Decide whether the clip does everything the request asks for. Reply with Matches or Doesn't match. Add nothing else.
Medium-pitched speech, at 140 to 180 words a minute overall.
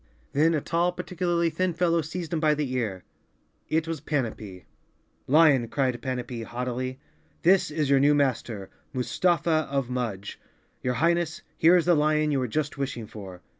Matches